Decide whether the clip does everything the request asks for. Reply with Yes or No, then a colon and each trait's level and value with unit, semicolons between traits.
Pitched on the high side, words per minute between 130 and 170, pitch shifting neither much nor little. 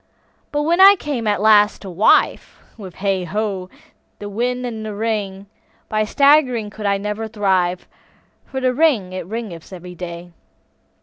Yes: high, 210 Hz; average, 150 wpm; average, 3.9 semitones